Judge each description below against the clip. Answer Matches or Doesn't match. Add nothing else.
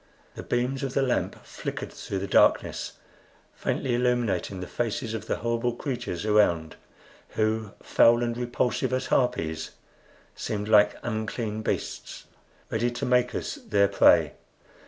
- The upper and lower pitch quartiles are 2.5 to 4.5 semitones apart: Matches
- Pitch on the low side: Matches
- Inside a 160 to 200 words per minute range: Doesn't match